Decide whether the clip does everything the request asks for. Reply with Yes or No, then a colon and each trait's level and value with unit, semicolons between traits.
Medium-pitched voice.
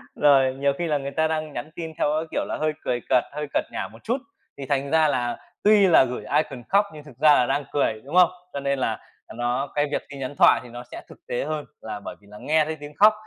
Yes: medium, 145 Hz